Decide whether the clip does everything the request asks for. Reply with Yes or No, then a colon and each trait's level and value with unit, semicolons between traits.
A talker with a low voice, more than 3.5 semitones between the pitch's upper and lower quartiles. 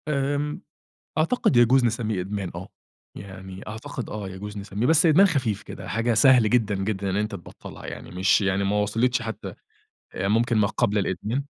Yes: low, 110 Hz; average, 4.0 semitones